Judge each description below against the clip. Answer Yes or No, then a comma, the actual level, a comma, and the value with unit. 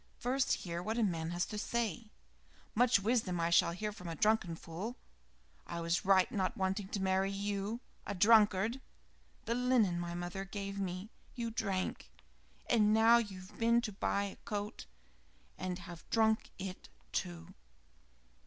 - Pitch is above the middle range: Yes, high, 200 Hz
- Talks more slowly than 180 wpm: Yes, average, 160 wpm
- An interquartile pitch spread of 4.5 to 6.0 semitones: No, average, 3.7 semitones